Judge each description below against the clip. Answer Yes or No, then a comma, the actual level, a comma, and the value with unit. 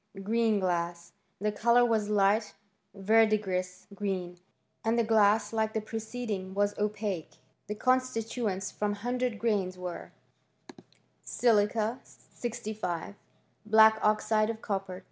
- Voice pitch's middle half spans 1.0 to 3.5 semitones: Yes, narrow, 2.4 semitones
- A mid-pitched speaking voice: No, high, 210 Hz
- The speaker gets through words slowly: Yes, slow, 110 wpm